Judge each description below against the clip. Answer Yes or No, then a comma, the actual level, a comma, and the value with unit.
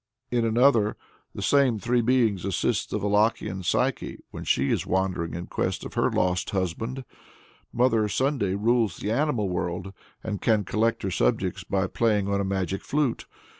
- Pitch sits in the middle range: No, low, 105 Hz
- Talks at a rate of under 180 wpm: Yes, average, 165 wpm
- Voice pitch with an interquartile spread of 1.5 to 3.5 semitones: No, average, 3.9 semitones